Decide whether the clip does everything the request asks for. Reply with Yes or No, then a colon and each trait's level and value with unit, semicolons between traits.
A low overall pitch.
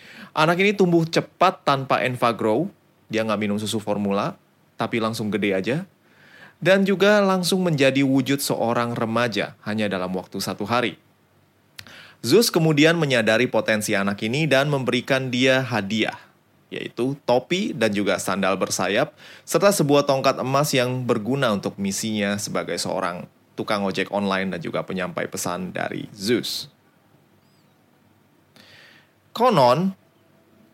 Yes: low, 125 Hz